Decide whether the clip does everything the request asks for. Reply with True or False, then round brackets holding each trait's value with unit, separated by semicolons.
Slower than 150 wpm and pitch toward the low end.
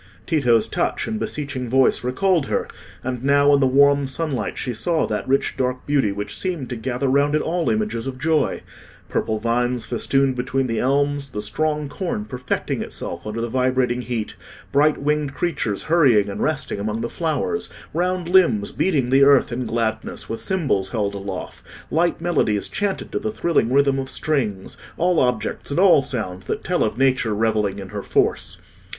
False (175 wpm; 130 Hz)